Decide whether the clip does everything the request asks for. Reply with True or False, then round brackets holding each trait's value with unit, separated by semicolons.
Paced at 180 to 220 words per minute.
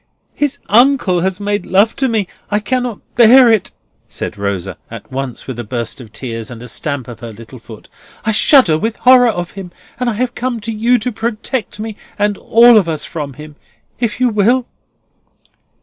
True (195 wpm)